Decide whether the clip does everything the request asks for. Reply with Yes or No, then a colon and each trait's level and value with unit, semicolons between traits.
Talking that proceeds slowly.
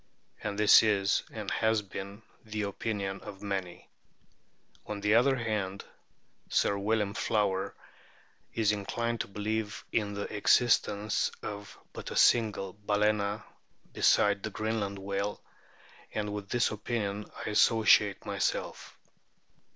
Yes: slow, 120 wpm